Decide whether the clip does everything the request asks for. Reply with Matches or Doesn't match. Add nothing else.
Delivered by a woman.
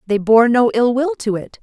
Matches